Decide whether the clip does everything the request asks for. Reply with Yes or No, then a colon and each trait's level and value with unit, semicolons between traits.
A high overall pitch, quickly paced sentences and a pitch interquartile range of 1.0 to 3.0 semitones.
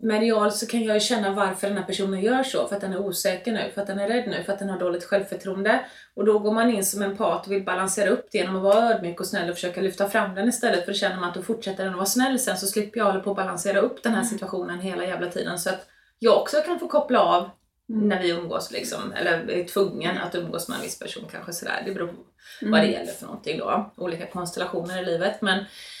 Yes: high, 200 Hz; fast, 275 wpm; narrow, 2.5 semitones